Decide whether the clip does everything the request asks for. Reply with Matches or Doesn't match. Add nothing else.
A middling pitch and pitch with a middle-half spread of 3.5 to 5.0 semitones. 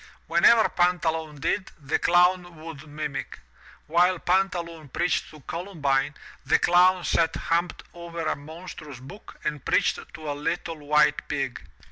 Doesn't match